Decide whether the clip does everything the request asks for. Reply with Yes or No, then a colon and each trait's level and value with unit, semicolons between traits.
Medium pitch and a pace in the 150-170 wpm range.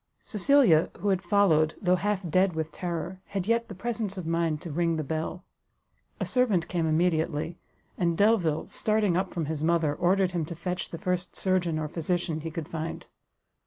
No: medium, 175 Hz; average, 185 wpm